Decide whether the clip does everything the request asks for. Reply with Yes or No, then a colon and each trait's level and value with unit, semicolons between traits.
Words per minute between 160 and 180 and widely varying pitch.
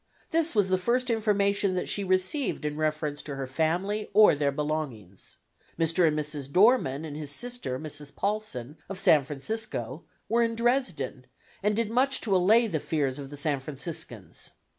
Yes: average, 170 wpm; wide, 6.7 semitones